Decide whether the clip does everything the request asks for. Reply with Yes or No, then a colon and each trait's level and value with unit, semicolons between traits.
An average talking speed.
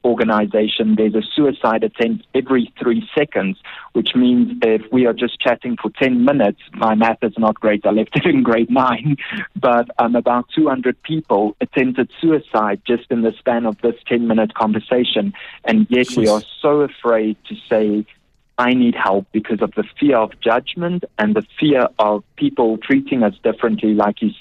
Yes: average, 180 wpm